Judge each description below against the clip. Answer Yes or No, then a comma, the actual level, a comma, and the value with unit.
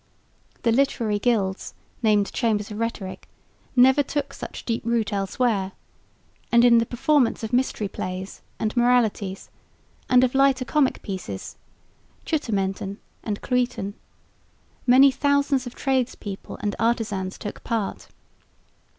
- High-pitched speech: Yes, high, 230 Hz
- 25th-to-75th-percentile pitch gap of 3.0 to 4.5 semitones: Yes, average, 3.9 semitones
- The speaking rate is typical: No, slow, 120 wpm